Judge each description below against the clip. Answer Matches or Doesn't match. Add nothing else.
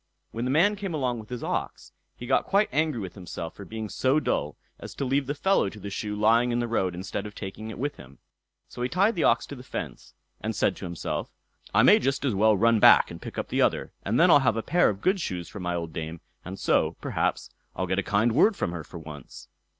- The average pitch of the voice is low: Matches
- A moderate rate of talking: Doesn't match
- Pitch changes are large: Matches